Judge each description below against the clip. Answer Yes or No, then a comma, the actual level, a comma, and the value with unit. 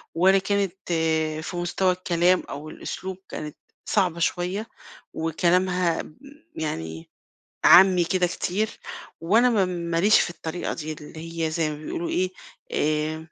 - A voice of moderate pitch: Yes, medium, 175 Hz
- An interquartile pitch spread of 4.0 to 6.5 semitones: No, average, 2.8 semitones